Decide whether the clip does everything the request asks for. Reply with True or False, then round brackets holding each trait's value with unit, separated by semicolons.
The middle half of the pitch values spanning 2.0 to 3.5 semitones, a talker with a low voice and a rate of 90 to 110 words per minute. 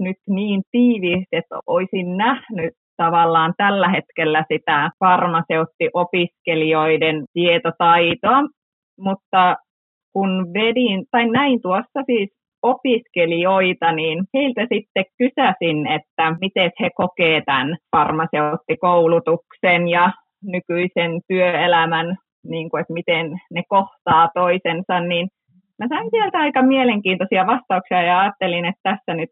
False (3.2 semitones; 180 Hz; 105 wpm)